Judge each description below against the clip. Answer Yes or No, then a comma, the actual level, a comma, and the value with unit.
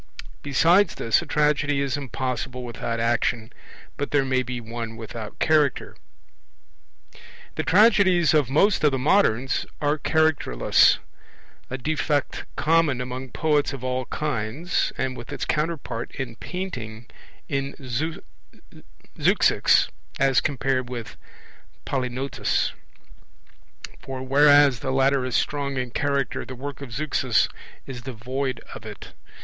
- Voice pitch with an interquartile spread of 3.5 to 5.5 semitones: No, average, 2.9 semitones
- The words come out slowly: Yes, slow, 120 wpm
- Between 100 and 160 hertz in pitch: Yes, low, 135 Hz